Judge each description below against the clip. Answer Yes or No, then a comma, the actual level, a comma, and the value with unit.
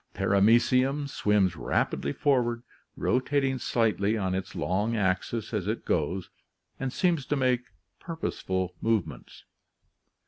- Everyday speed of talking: No, slow, 110 wpm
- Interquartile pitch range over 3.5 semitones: Yes, average, 5.3 semitones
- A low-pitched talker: Yes, low, 115 Hz